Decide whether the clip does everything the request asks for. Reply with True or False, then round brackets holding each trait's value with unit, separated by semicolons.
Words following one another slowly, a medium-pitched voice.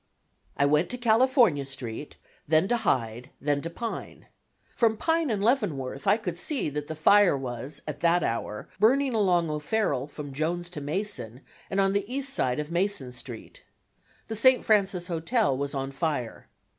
False (170 wpm; 170 Hz)